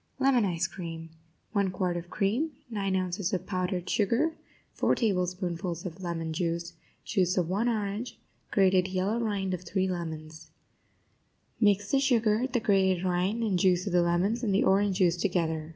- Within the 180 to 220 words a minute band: No, average, 165 wpm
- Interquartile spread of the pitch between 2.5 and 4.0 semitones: Yes, average, 2.8 semitones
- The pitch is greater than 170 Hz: Yes, medium, 185 Hz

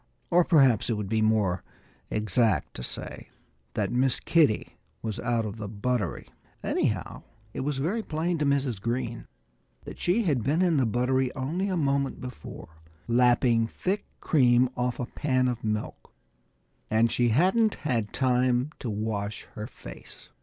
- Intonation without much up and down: No, average, 4.1 semitones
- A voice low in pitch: Yes, low, 125 Hz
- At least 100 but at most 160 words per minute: Yes, average, 155 wpm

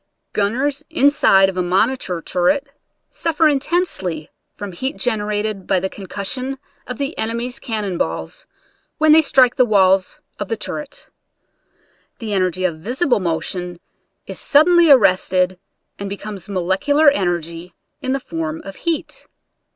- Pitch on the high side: Yes, high, 205 Hz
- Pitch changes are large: Yes, wide, 6.7 semitones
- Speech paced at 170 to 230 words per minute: No, average, 140 wpm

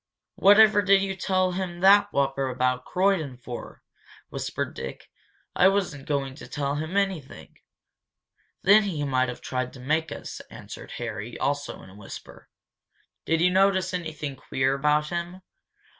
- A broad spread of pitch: Yes, wide, 5.8 semitones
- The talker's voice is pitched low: No, medium, 160 Hz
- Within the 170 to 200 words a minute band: No, average, 155 wpm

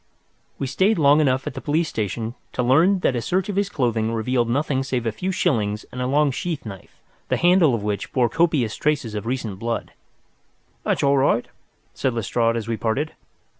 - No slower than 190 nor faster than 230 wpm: Yes, average, 200 wpm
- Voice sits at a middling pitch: No, low, 130 Hz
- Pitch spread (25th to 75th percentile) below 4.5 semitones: No, average, 4.8 semitones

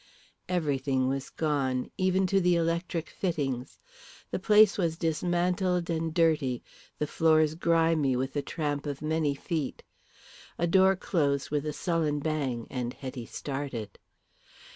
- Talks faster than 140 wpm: No, slow, 135 wpm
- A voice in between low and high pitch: Yes, medium, 155 Hz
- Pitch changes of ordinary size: Yes, average, 3.6 semitones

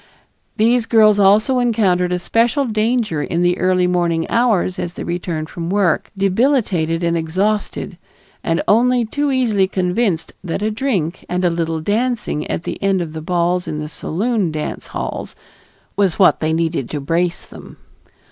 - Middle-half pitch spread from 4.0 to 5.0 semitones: Yes, average, 4.6 semitones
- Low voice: No, medium, 185 Hz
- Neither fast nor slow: Yes, average, 165 wpm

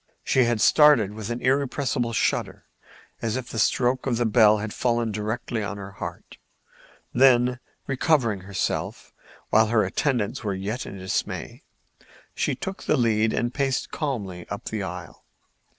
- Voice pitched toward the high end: No, low, 115 Hz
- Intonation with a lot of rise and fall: No, average, 3.5 semitones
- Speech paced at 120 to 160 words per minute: Yes, average, 150 wpm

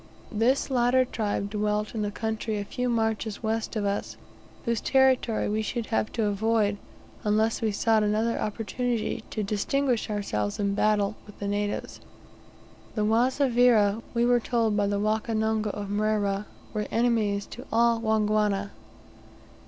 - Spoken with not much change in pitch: Yes, narrow, 2.0 semitones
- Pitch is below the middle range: No, high, 215 Hz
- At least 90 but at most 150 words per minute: Yes, average, 145 wpm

